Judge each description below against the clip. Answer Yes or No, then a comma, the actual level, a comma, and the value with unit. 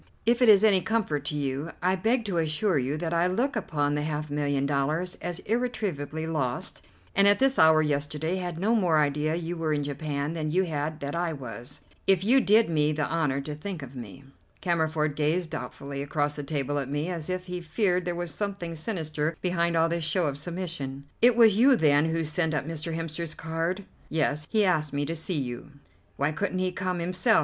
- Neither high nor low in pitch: Yes, medium, 160 Hz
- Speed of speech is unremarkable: No, fast, 210 wpm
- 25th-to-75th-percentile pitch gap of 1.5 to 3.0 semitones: No, average, 3.7 semitones